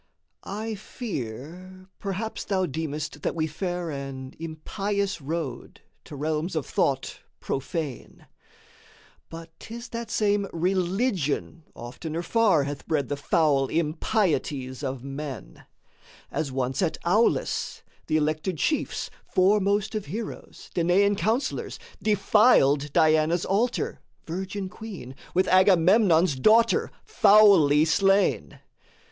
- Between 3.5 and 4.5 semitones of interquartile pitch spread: No, average, 5.3 semitones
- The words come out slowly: Yes, slow, 105 wpm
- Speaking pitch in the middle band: Yes, medium, 170 Hz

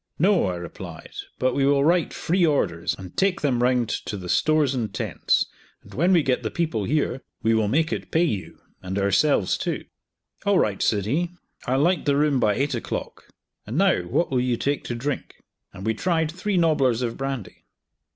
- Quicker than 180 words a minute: Yes, average, 200 wpm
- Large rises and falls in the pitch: Yes, wide, 6.4 semitones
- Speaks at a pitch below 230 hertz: Yes, low, 135 Hz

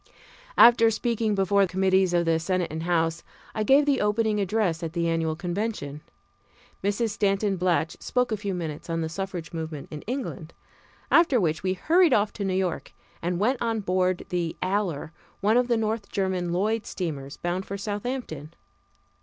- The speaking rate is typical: Yes, average, 170 wpm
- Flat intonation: No, average, 4.3 semitones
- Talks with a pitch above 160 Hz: Yes, high, 190 Hz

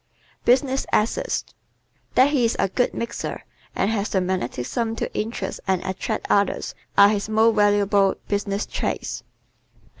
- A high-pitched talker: Yes, high, 210 Hz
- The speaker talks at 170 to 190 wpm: No, average, 145 wpm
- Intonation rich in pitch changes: No, average, 2.7 semitones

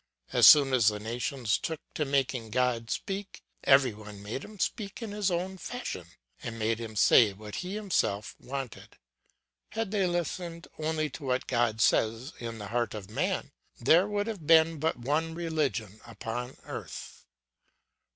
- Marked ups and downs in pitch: Yes, wide, 7.1 semitones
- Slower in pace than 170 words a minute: Yes, average, 160 wpm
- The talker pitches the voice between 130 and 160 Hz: Yes, low, 135 Hz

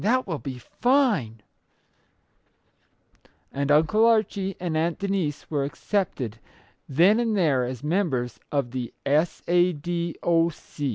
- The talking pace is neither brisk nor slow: No, slow, 130 wpm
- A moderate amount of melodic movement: No, wide, 5.9 semitones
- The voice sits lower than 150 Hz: No, medium, 165 Hz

